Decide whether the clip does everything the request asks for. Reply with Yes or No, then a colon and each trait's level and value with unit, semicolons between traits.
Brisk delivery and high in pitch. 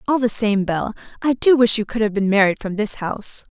Yes: fast, 255 wpm; high, 215 Hz